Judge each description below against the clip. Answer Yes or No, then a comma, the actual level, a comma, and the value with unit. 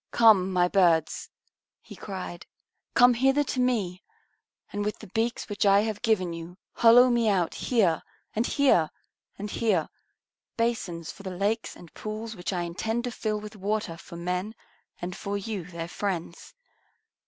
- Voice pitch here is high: Yes, high, 205 Hz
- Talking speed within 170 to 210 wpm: No, average, 160 wpm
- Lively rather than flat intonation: No, average, 4.1 semitones